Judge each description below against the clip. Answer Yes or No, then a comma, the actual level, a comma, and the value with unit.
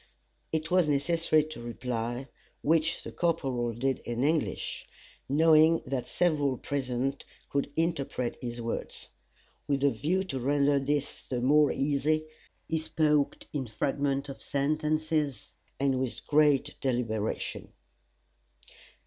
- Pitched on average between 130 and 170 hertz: Yes, medium, 140 Hz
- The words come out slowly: Yes, slow, 120 wpm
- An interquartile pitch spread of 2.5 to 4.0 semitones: Yes, average, 3.1 semitones